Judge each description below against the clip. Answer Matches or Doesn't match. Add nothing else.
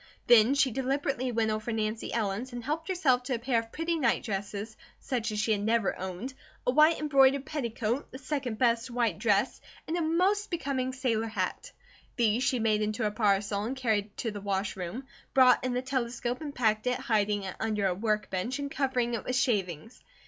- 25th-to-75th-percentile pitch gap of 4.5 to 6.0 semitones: Doesn't match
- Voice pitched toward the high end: Matches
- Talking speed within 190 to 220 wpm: Matches